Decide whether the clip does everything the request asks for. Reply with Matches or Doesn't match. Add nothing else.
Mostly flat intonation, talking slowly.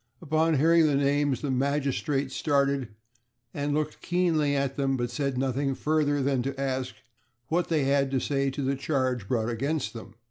Doesn't match